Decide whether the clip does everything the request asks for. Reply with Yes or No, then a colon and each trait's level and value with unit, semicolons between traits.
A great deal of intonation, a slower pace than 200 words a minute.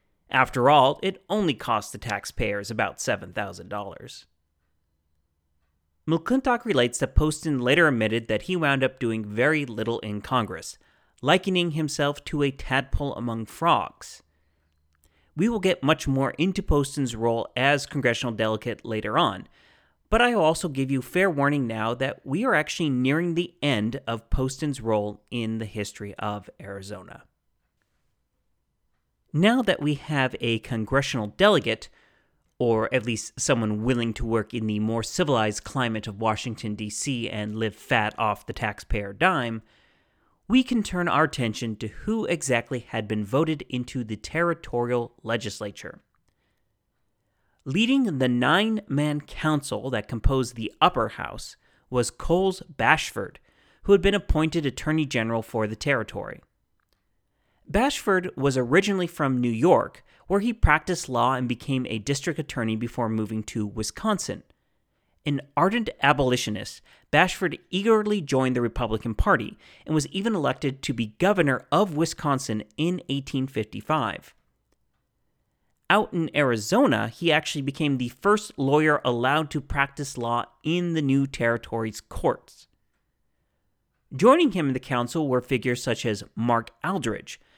Yes: wide, 5.7 semitones; average, 140 wpm